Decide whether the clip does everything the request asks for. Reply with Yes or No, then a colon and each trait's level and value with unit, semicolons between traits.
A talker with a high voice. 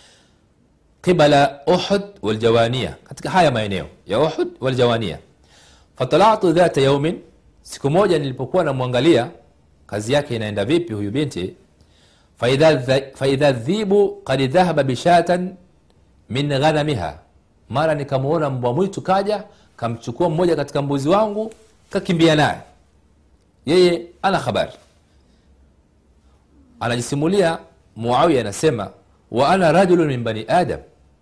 No: medium, 140 Hz